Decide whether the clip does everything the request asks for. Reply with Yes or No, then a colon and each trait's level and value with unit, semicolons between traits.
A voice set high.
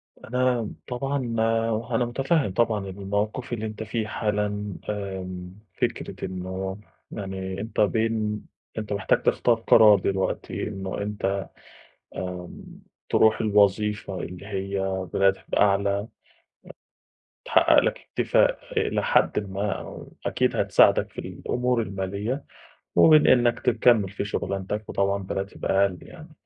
No: low, 105 Hz